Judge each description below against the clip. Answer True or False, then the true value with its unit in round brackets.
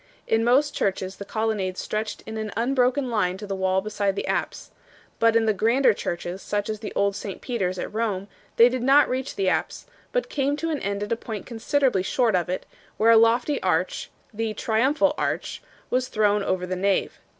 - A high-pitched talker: True (220 Hz)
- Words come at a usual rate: False (215 wpm)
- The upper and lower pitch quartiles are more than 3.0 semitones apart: True (4.0 semitones)